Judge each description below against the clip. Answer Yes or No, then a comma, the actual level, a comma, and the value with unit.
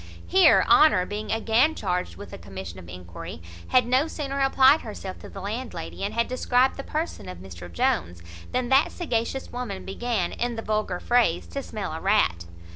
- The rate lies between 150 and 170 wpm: No, average, 185 wpm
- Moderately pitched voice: No, high, 220 Hz